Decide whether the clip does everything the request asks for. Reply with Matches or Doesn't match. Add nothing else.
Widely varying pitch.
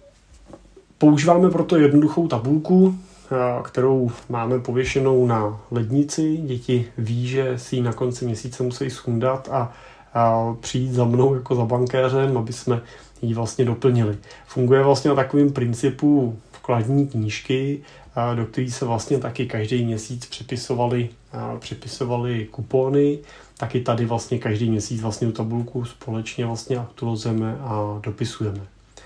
Doesn't match